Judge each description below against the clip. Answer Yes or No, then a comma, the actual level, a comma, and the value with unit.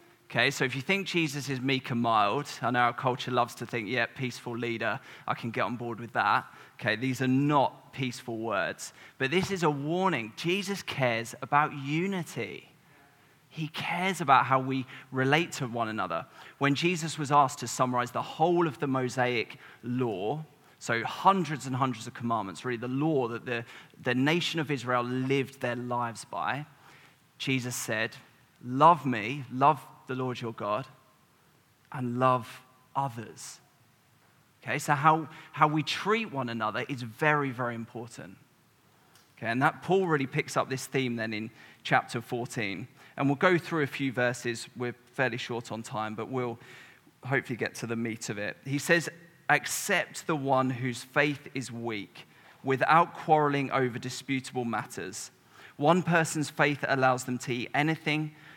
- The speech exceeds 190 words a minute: No, average, 165 wpm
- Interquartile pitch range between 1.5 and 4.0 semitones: Yes, average, 3.4 semitones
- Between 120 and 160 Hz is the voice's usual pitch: Yes, low, 130 Hz